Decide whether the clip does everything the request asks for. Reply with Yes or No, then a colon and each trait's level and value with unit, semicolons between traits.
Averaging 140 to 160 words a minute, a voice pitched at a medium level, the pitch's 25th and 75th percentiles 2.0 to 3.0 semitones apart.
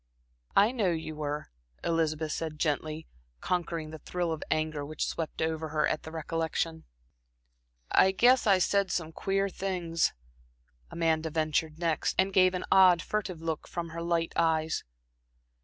Yes: average, 150 wpm; medium, 165 Hz; narrow, 2.4 semitones